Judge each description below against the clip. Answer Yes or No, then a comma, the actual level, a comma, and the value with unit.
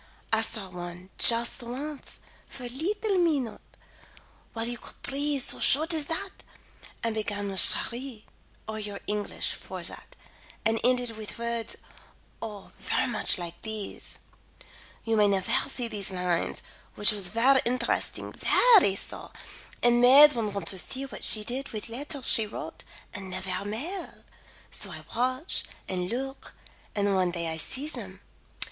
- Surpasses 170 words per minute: No, average, 155 wpm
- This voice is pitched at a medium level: No, high, 230 Hz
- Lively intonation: No, average, 4.7 semitones